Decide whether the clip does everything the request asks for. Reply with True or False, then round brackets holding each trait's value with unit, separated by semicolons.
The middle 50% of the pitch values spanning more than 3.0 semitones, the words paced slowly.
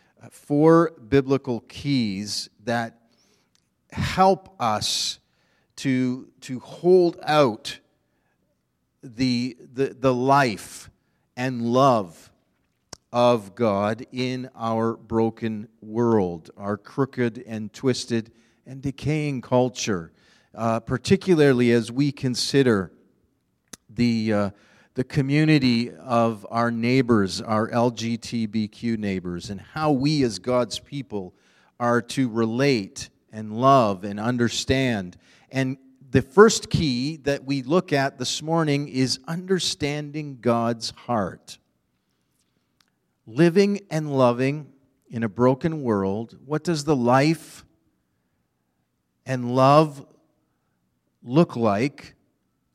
True (3.6 semitones; 100 wpm)